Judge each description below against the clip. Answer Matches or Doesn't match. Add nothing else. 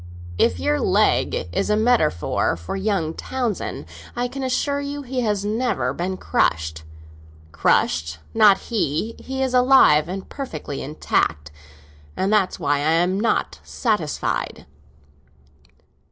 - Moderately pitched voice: Doesn't match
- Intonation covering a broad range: Matches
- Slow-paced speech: Matches